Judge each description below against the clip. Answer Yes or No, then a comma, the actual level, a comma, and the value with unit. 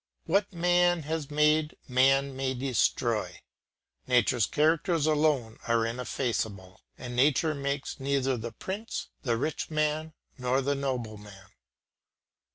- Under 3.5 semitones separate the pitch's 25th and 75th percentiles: No, average, 4.0 semitones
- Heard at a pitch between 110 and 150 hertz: Yes, medium, 140 Hz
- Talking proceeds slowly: Yes, slow, 115 wpm